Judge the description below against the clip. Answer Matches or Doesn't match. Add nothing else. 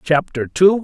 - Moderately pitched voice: Matches